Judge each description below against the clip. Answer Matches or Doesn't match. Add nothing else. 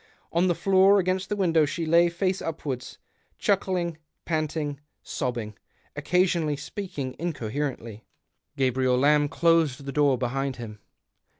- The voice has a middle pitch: Matches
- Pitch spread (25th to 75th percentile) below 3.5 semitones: Doesn't match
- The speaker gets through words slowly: Matches